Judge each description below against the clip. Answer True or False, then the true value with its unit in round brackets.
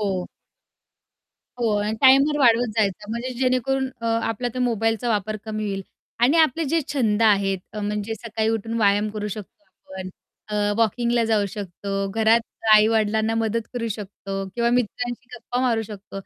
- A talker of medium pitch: False (225 Hz)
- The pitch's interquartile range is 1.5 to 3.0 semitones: True (2.6 semitones)